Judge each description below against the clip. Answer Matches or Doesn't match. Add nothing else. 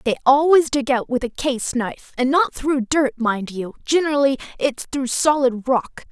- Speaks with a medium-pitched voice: Doesn't match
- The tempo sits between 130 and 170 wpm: Doesn't match